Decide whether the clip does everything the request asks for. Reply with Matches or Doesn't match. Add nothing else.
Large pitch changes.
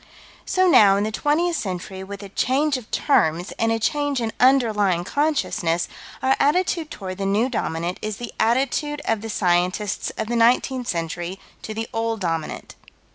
Matches